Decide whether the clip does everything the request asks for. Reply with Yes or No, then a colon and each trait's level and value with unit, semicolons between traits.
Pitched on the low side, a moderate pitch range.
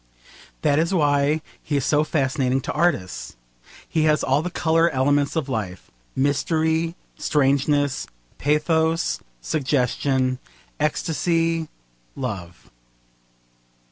No: medium, 145 Hz; average, 3.2 semitones